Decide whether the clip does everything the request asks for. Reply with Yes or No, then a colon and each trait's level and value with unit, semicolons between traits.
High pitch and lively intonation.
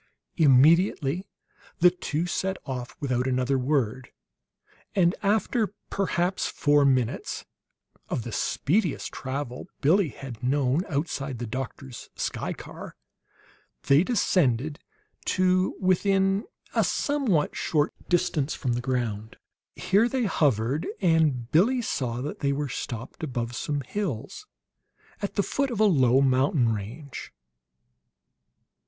No: medium, 145 Hz; wide, 6.4 semitones